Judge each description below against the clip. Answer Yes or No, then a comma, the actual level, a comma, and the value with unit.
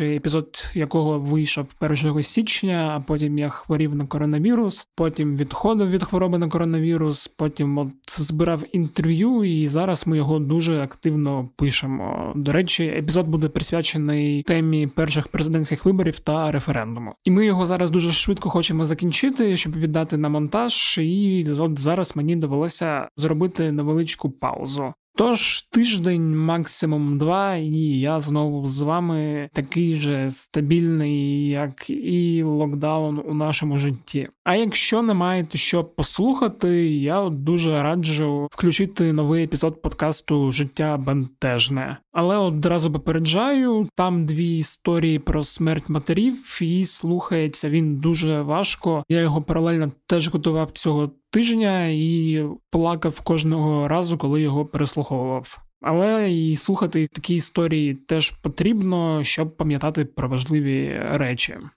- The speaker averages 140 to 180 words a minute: No, average, 130 wpm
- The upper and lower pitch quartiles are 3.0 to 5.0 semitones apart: No, narrow, 2.5 semitones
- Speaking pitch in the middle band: Yes, medium, 160 Hz